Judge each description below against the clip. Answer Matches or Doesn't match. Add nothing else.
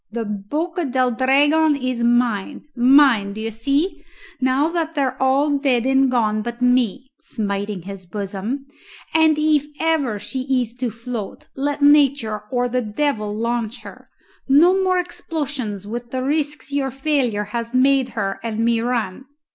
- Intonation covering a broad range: Doesn't match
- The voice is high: Matches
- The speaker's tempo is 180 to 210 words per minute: Doesn't match